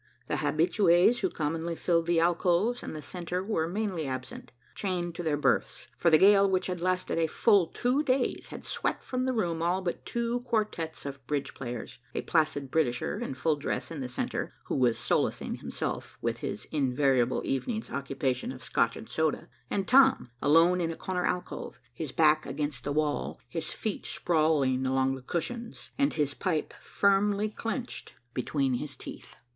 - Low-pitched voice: No, medium, 165 Hz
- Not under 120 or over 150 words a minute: No, average, 175 wpm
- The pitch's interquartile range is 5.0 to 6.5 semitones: Yes, wide, 5.5 semitones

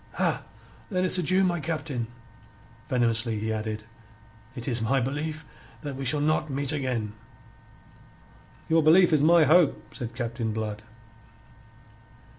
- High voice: No, low, 135 Hz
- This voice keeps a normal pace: No, slow, 130 wpm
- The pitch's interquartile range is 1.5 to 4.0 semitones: No, average, 5.3 semitones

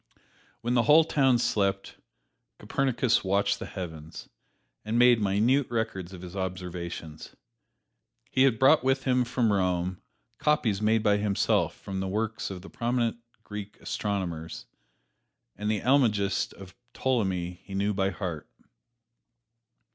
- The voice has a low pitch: Yes, low, 105 Hz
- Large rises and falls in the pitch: No, average, 4.2 semitones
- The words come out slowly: Yes, slow, 130 wpm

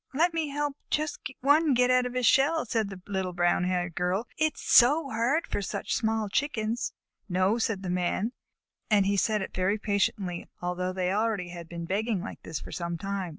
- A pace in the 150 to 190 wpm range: No, average, 200 wpm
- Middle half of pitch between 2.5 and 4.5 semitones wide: No, wide, 5.5 semitones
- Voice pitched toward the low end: No, high, 210 Hz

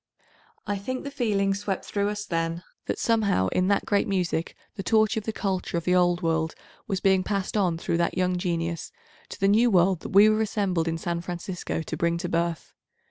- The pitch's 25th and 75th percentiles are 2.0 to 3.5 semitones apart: Yes, average, 3.2 semitones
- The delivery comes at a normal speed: No, fast, 215 wpm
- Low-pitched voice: No, medium, 185 Hz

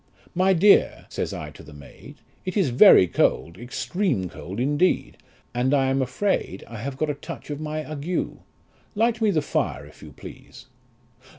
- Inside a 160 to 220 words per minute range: Yes, average, 175 wpm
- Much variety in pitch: Yes, wide, 7.1 semitones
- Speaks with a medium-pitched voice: Yes, medium, 145 Hz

